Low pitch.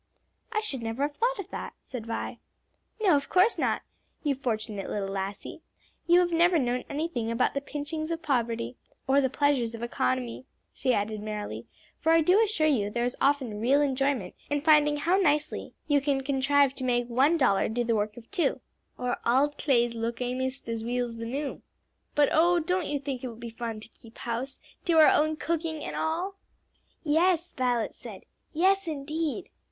No: very high, 275 Hz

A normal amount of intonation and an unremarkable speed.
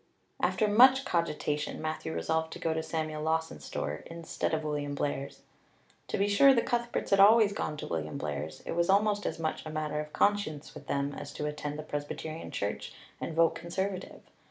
Yes: average, 4.8 semitones; average, 190 wpm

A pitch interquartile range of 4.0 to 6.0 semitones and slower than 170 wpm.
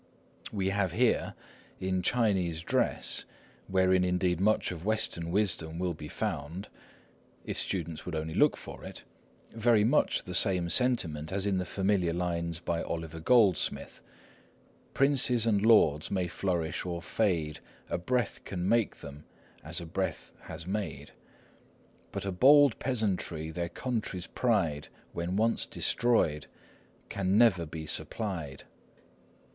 Yes: average, 4.3 semitones; slow, 135 wpm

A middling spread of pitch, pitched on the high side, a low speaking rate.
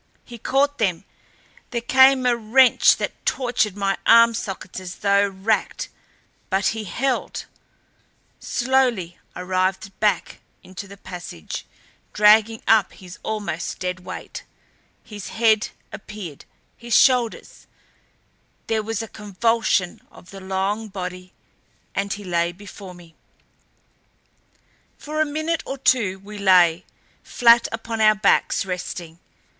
Yes: average, 3.8 semitones; high, 205 Hz; slow, 125 wpm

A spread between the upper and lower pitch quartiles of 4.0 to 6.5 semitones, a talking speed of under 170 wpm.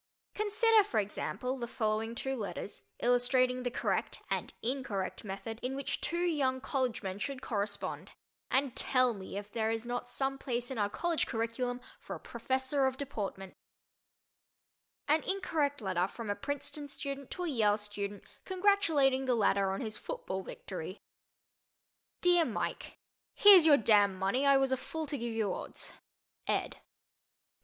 Yes: average, 4.8 semitones; average, 155 wpm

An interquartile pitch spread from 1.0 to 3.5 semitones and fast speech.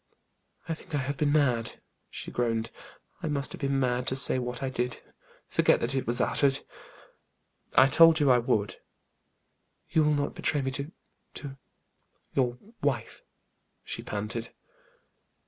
No: average, 2.7 semitones; average, 150 wpm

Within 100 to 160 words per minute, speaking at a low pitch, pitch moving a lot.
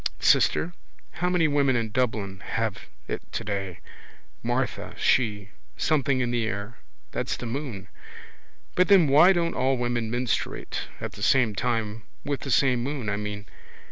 No: average, 150 wpm; low, 120 Hz; average, 4.8 semitones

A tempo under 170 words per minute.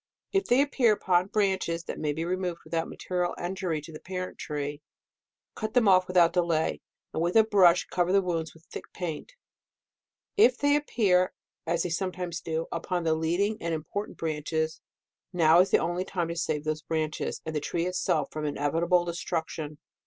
No: average, 180 wpm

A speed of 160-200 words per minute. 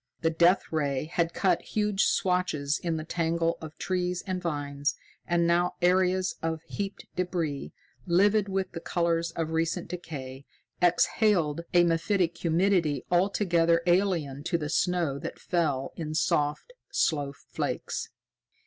No: slow, 135 wpm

